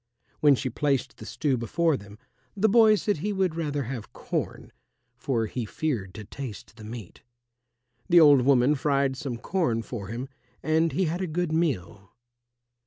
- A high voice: No, medium, 140 Hz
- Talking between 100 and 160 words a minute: No, average, 170 wpm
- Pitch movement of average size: No, wide, 5.8 semitones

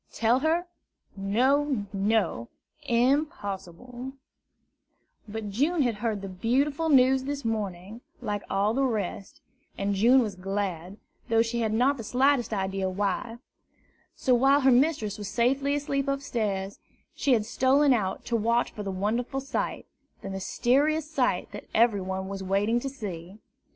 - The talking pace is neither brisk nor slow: Yes, average, 145 wpm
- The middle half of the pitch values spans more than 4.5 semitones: Yes, average, 5.1 semitones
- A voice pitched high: Yes, high, 230 Hz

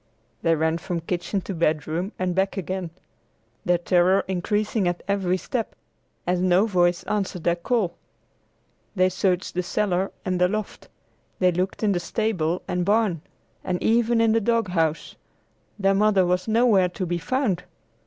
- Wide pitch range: No, average, 2.8 semitones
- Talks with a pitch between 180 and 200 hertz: Yes, medium, 185 Hz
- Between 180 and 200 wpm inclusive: No, average, 160 wpm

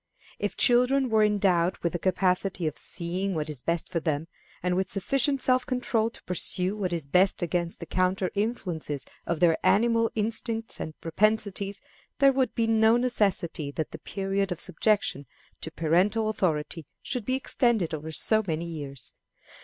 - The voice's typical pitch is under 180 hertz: No, high, 190 Hz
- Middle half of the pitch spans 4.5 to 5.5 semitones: Yes, average, 4.8 semitones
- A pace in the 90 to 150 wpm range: No, average, 165 wpm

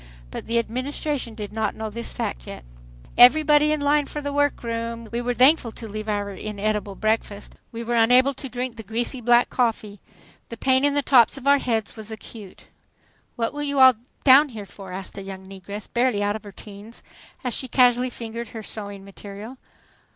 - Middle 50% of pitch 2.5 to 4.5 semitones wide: Yes, average, 3.6 semitones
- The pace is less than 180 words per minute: No, average, 195 wpm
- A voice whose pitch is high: Yes, high, 230 Hz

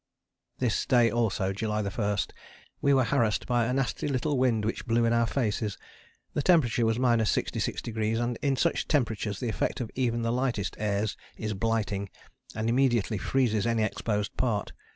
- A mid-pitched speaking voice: No, low, 115 Hz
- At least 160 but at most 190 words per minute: Yes, average, 165 wpm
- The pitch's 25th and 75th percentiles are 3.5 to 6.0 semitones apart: No, average, 2.8 semitones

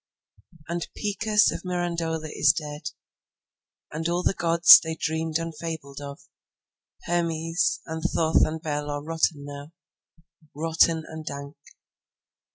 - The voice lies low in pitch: No, medium, 160 Hz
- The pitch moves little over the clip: Yes, narrow, 2.1 semitones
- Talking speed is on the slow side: Yes, slow, 110 wpm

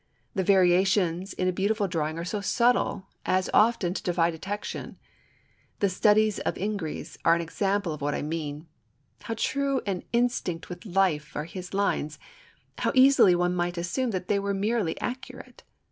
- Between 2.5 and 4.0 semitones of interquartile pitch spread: Yes, average, 3.5 semitones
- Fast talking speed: No, average, 170 wpm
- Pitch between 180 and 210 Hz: Yes, high, 190 Hz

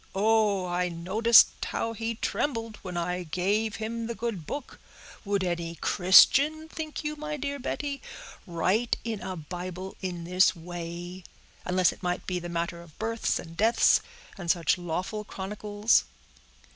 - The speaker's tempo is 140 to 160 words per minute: Yes, average, 150 wpm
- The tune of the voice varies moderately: Yes, average, 4.4 semitones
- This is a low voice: No, high, 190 Hz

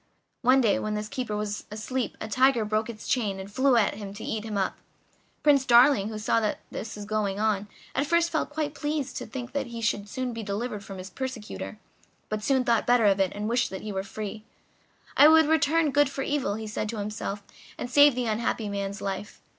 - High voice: Yes, high, 220 Hz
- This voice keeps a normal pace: No, fast, 220 wpm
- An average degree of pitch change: Yes, average, 4.1 semitones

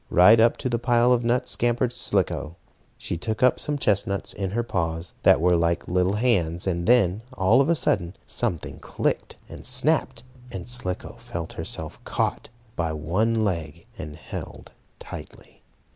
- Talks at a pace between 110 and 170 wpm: Yes, average, 160 wpm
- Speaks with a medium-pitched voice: No, low, 100 Hz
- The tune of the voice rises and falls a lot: Yes, wide, 5.7 semitones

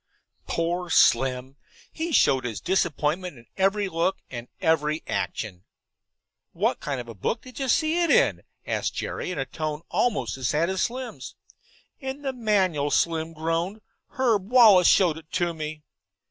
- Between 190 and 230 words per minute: No, average, 160 wpm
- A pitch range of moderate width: No, wide, 6.2 semitones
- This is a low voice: No, medium, 170 Hz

